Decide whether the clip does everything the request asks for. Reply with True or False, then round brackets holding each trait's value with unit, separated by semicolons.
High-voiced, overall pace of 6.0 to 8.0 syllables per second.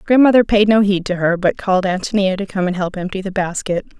True (195 Hz; 6.1 syllables/s)